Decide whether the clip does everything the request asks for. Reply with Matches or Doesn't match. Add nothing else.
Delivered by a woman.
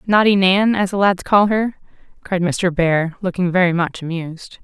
Matches